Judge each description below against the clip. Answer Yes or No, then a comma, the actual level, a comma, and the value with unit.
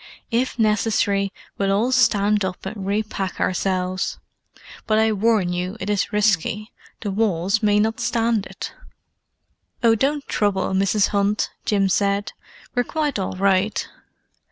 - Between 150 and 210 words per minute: No, average, 140 wpm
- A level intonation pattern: Yes, narrow, 2.3 semitones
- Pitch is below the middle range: No, high, 205 Hz